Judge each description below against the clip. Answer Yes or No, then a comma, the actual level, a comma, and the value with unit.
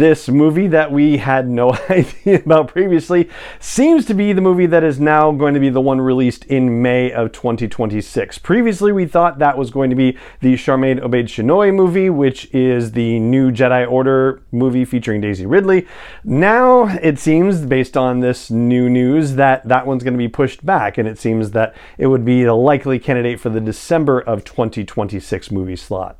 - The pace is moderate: Yes, average, 190 wpm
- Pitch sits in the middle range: No, low, 130 Hz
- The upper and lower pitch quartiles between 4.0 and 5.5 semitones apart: Yes, average, 4.5 semitones